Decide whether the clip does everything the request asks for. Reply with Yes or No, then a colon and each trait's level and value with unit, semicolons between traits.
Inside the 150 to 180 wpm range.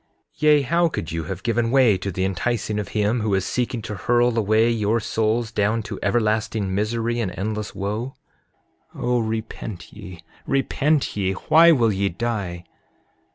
Yes: average, 170 wpm